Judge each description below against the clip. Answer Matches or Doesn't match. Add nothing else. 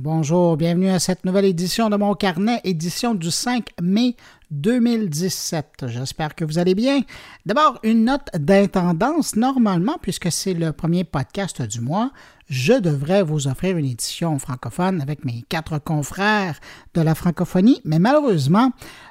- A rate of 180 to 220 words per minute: Doesn't match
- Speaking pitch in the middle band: Matches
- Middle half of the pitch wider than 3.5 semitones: Matches